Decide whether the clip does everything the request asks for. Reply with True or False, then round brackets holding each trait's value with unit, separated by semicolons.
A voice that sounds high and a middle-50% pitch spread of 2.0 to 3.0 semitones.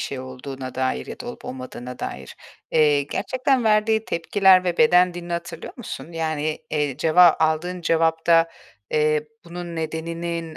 False (165 Hz; 2.7 semitones)